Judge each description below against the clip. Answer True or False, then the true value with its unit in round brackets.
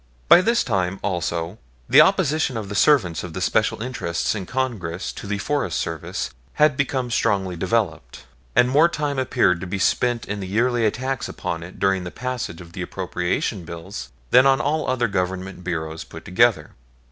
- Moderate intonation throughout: False (6.1 semitones)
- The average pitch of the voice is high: False (100 Hz)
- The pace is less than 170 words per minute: False (180 wpm)